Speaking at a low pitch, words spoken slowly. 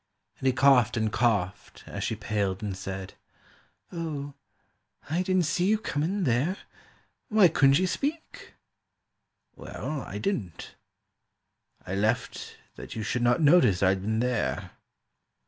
Yes: low, 125 Hz; slow, 130 wpm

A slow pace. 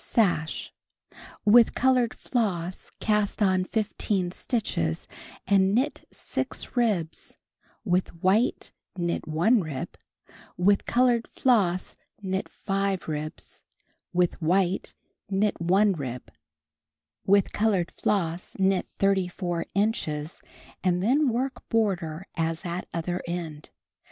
Yes: slow, 105 wpm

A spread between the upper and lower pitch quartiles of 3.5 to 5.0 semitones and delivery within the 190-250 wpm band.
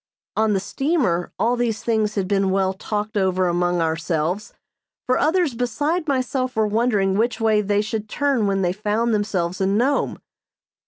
No: average, 4.1 semitones; average, 165 wpm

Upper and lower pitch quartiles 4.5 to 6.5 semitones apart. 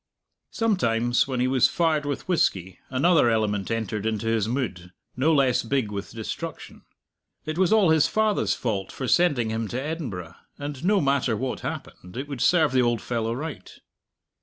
Yes: wide, 5.5 semitones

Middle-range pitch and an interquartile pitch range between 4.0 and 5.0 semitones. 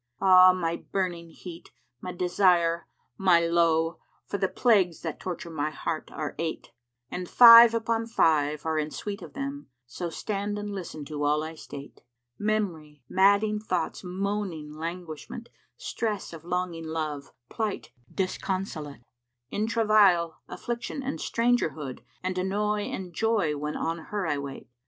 Yes: medium, 180 Hz; average, 4.5 semitones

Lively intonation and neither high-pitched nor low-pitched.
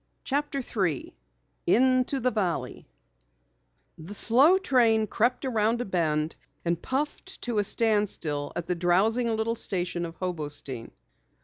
No: wide, 6.3 semitones; high, 215 Hz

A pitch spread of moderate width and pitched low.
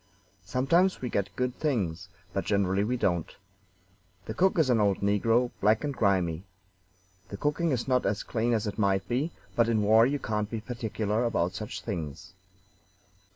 Yes: average, 4.1 semitones; low, 110 Hz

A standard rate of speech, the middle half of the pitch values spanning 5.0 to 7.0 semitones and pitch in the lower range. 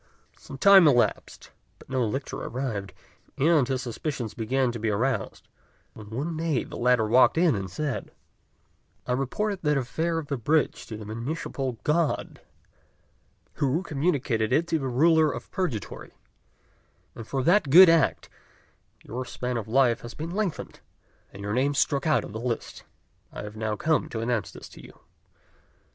Yes: average, 165 wpm; average, 5.3 semitones; low, 130 Hz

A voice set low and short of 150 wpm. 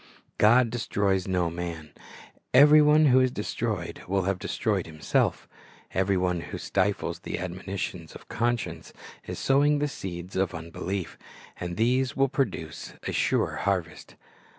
Yes: very low, 95 Hz; average, 140 wpm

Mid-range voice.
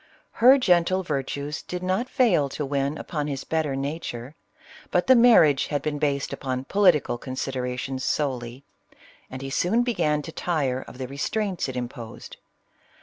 Yes: medium, 145 Hz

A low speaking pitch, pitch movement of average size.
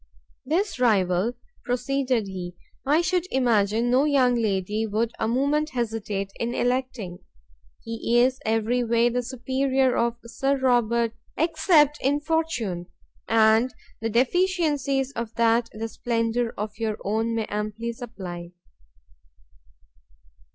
No: high, 235 Hz; average, 3.2 semitones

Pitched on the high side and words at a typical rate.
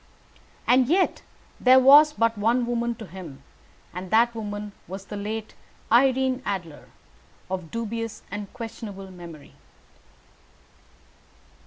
No: high, 225 Hz; slow, 115 wpm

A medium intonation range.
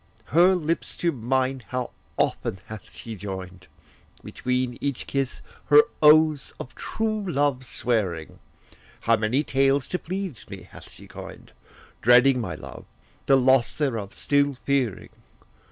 Yes: average, 3.9 semitones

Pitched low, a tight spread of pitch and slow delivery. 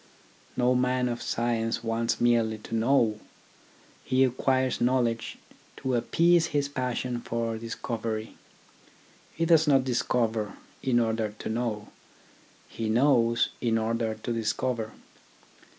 Yes: low, 120 Hz; narrow, 2.1 semitones; slow, 120 wpm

